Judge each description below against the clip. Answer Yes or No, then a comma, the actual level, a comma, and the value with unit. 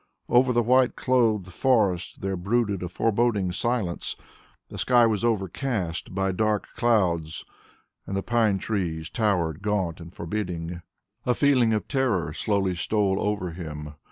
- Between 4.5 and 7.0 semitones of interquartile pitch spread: Yes, average, 4.9 semitones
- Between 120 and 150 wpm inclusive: Yes, average, 140 wpm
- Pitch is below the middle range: Yes, low, 100 Hz